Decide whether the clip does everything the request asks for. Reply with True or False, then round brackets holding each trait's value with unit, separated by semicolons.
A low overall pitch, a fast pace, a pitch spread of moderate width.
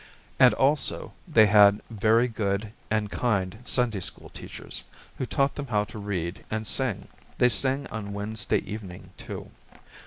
False (110 Hz; 150 wpm; 3.2 semitones)